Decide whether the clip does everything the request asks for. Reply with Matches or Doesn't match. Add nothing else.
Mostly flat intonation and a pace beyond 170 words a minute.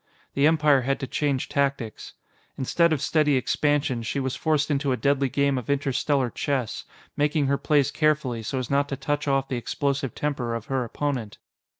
Matches